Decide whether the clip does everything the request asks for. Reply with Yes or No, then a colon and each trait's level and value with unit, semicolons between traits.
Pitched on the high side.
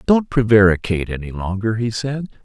No: low, 110 Hz